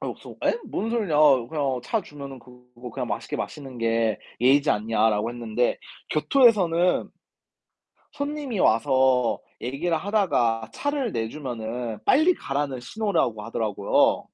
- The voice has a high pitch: No, low, 130 Hz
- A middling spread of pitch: No, wide, 7.8 semitones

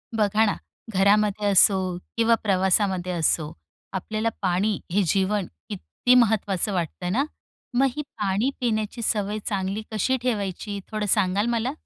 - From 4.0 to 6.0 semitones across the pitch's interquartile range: No, narrow, 2.4 semitones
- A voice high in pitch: Yes, high, 205 Hz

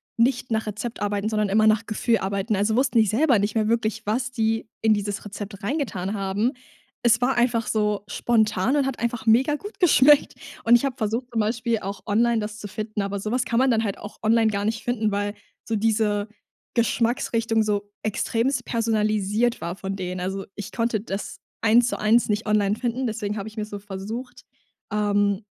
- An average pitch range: No, narrow, 2.3 semitones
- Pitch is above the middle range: Yes, high, 220 Hz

